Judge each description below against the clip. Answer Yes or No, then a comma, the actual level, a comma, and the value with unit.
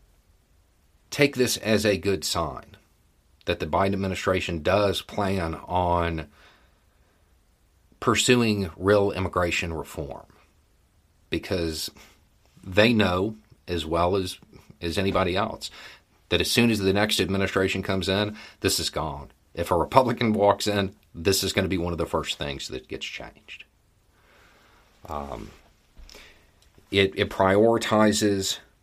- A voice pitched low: Yes, very low, 95 Hz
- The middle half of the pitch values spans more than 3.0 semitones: Yes, average, 3.4 semitones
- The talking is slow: Yes, slow, 125 wpm